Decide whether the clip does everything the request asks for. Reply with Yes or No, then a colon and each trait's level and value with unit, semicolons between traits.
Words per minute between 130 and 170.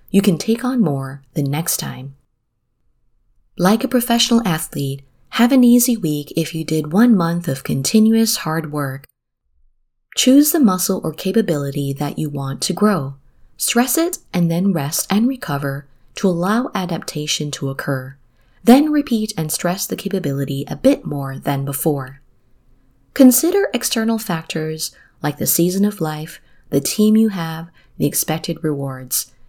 Yes: average, 150 wpm